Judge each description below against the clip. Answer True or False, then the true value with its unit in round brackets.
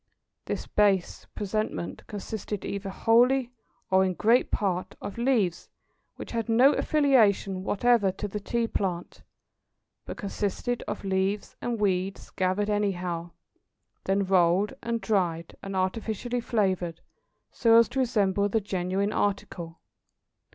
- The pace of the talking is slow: True (125 wpm)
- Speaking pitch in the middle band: False (200 Hz)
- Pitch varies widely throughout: False (3.2 semitones)